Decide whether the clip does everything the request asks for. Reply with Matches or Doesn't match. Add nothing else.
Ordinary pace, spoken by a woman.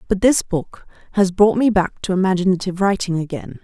Matches